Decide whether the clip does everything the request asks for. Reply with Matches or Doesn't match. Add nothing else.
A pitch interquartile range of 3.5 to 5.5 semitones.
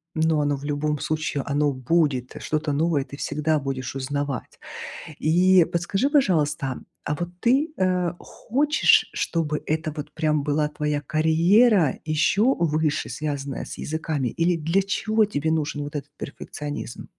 Doesn't match